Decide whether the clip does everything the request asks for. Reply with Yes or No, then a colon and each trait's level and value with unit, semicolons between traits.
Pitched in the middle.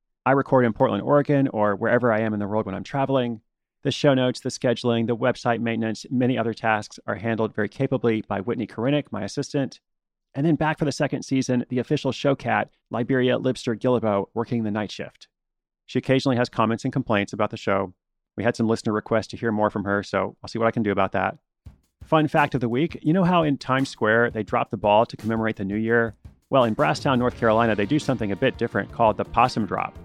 No: low, 120 Hz